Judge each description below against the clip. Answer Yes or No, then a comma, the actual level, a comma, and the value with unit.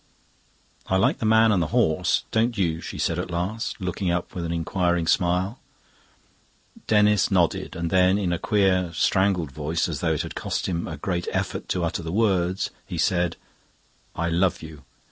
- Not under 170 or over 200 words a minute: Yes, average, 185 wpm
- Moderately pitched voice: No, very low, 90 Hz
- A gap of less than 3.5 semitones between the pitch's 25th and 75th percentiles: Yes, narrow, 2.5 semitones